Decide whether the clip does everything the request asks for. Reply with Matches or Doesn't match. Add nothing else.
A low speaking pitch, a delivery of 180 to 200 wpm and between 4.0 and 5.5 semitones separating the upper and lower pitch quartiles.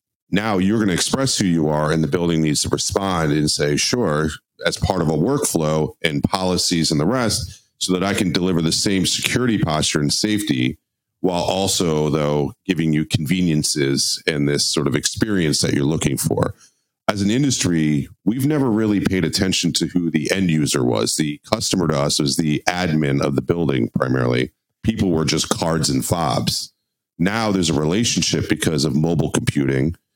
Matches